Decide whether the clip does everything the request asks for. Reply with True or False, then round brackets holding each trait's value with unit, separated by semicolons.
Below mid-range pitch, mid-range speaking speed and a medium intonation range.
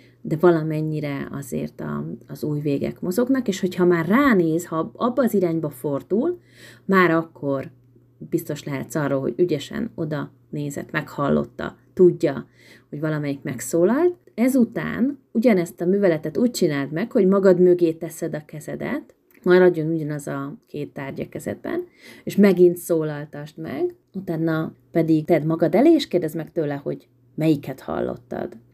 False (165 Hz; 140 wpm; 4.3 semitones)